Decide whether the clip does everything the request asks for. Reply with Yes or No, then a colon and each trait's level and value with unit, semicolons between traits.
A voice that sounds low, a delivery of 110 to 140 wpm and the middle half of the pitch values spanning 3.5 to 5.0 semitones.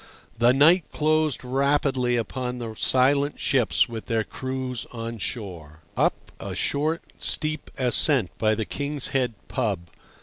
Yes: low, 125 Hz; slow, 135 wpm; average, 3.8 semitones